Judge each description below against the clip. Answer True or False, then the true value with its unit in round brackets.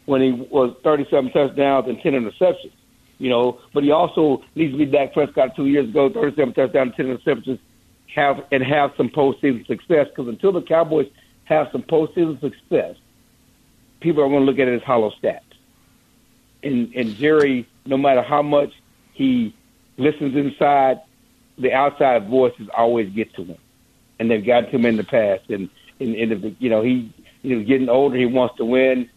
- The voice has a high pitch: False (135 Hz)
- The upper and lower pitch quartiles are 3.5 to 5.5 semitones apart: False (3.1 semitones)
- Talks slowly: False (185 wpm)